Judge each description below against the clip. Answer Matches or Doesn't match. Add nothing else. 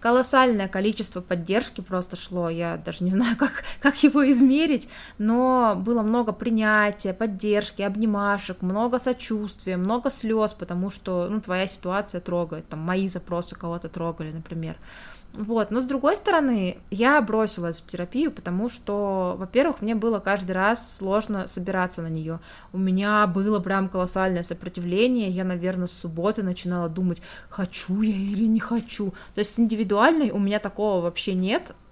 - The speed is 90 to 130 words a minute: Doesn't match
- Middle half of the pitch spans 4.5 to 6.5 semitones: Doesn't match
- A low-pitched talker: Doesn't match